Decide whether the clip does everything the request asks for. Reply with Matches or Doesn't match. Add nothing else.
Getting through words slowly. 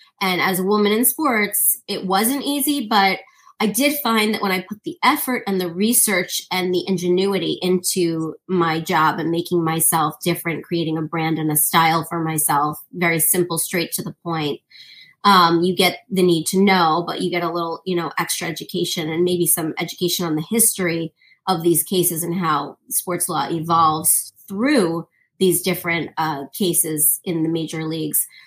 Doesn't match